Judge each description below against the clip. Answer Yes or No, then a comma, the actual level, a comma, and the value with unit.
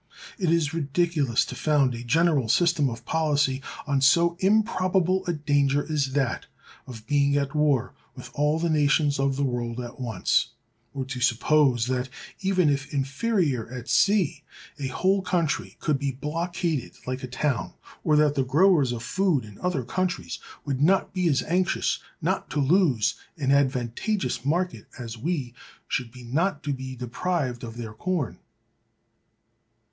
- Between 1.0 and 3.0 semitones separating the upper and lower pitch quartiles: No, average, 4.8 semitones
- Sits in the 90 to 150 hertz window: Yes, medium, 140 Hz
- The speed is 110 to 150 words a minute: No, average, 160 wpm